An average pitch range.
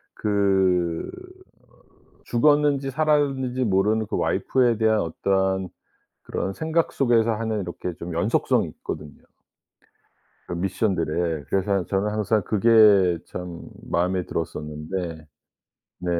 Yes: average, 4.5 semitones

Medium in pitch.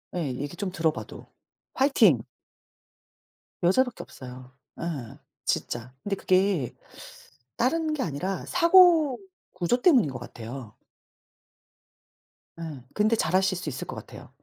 Yes: medium, 180 Hz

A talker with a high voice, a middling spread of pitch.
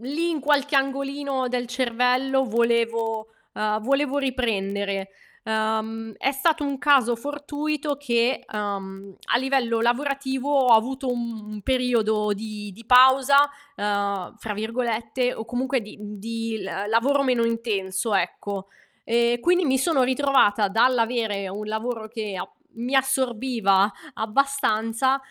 Yes: high, 235 Hz; average, 3.6 semitones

